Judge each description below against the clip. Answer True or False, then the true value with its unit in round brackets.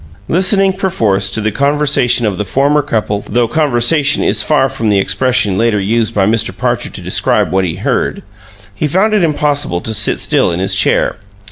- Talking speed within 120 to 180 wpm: False (190 wpm)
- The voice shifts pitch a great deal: True (6.1 semitones)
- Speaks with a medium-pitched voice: False (120 Hz)